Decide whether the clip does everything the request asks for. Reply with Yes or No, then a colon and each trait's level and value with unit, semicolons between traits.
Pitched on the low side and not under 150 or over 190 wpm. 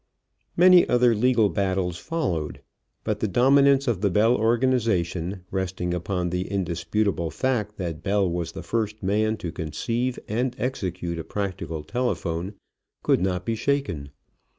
No: low, 100 Hz; average, 140 wpm